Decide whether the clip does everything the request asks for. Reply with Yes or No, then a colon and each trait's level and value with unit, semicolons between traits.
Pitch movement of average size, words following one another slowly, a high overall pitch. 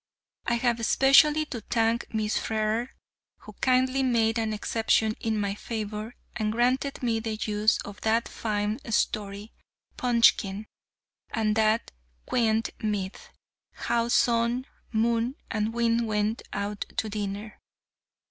No: narrow, 1.8 semitones; slow, 125 wpm; high, 225 Hz